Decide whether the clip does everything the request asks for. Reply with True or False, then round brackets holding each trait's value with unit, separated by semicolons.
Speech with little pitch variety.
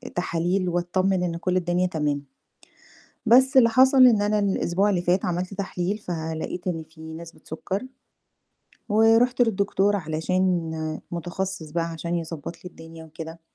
False (3.4 semitones)